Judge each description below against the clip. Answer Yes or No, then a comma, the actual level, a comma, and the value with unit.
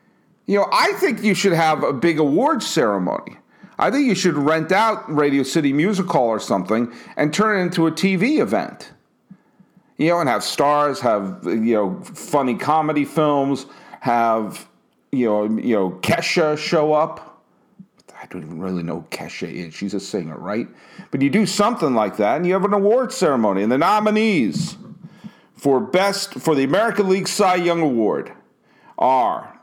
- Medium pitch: Yes, medium, 160 Hz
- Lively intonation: Yes, wide, 6.2 semitones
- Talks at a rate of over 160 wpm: Yes, average, 170 wpm